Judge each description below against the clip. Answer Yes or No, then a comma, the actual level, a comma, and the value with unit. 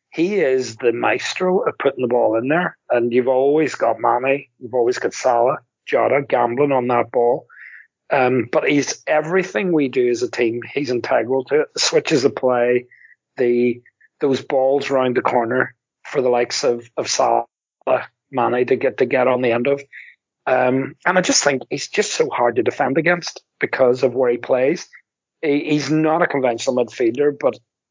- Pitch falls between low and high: No, low, 130 Hz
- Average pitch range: Yes, average, 4.1 semitones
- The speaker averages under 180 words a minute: No, average, 185 wpm